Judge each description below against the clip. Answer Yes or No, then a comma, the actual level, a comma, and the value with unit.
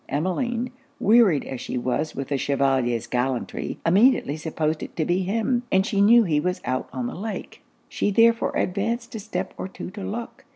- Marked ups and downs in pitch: Yes, wide, 8.1 semitones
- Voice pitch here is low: No, medium, 185 Hz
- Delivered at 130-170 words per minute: No, average, 190 wpm